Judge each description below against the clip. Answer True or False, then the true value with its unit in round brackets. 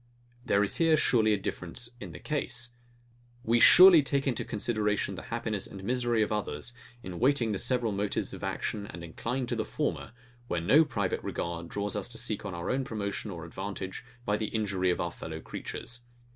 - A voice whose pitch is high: False (105 Hz)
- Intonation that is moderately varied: True (4.0 semitones)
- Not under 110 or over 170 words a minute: False (190 wpm)